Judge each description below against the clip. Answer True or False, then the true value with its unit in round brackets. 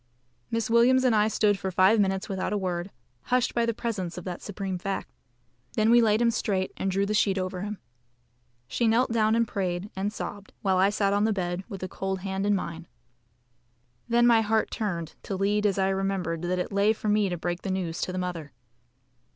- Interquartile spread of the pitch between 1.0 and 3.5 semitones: True (2.7 semitones)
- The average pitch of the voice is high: True (195 Hz)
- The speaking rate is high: True (215 wpm)